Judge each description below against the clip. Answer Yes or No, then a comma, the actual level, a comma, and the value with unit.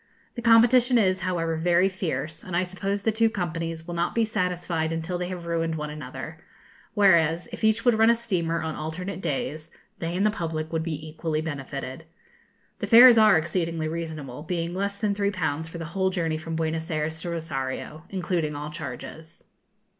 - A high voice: No, medium, 170 Hz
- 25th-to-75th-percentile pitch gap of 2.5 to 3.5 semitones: Yes, average, 3.2 semitones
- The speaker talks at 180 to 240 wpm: Yes, average, 185 wpm